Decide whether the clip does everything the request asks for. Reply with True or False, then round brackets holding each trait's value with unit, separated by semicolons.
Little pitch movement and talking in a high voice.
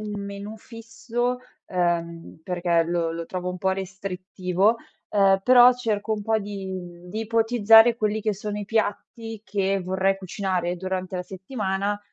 False (3.1 semitones; 195 Hz)